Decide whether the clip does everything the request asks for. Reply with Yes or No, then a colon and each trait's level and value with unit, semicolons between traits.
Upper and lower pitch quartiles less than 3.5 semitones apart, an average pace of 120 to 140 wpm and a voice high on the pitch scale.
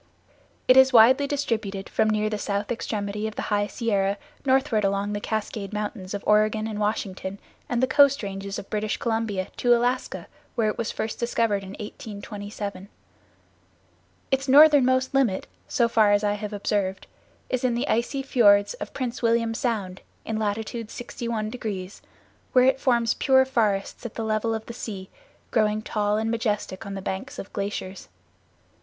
No: average, 2.8 semitones; average, 165 wpm; high, 215 Hz